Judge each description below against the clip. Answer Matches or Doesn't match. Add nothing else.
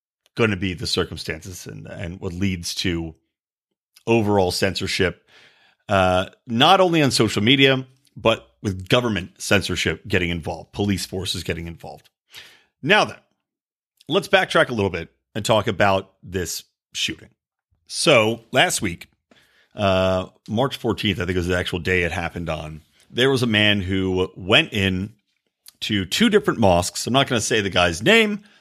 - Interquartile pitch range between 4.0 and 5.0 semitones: Matches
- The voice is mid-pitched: Doesn't match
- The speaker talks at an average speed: Matches